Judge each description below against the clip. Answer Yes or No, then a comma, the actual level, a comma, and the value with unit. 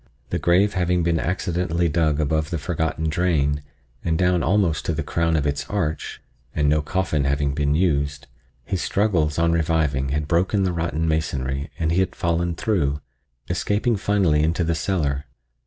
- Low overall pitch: Yes, very low, 80 Hz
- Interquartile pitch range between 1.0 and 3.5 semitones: Yes, average, 3.0 semitones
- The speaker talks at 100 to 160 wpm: No, average, 170 wpm